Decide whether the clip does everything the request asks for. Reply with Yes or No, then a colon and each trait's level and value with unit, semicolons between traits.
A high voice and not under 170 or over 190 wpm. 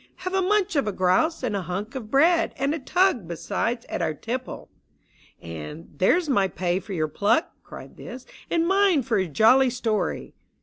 No: high, 240 Hz; fast, 205 wpm